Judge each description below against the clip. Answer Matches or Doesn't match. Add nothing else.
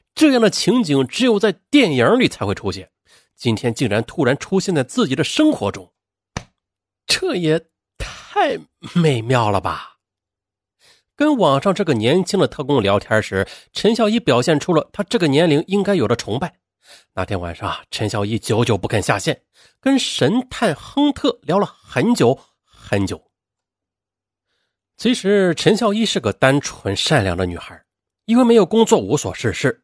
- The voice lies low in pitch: Doesn't match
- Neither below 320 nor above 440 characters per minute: Doesn't match